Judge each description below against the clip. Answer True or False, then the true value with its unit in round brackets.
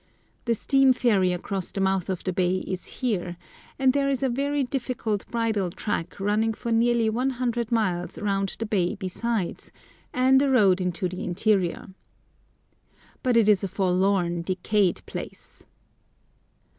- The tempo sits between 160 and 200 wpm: False (145 wpm)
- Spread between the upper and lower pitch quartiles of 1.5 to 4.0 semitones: False (4.4 semitones)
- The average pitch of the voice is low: False (210 Hz)